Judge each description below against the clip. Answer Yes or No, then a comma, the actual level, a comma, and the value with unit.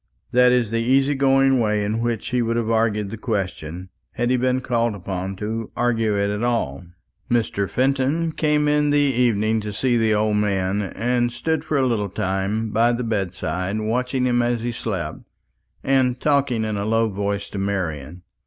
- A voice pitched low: Yes, low, 115 Hz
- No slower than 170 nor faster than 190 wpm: Yes, average, 185 wpm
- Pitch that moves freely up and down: No, average, 3.6 semitones